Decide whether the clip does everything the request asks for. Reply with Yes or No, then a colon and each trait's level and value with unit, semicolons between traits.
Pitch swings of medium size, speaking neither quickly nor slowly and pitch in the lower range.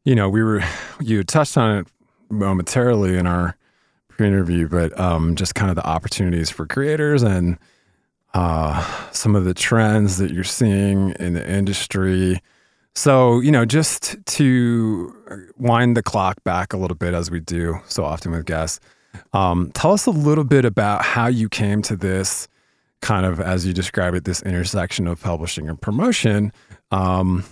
Yes: average, 4.0 semitones; average, 170 wpm; very low, 95 Hz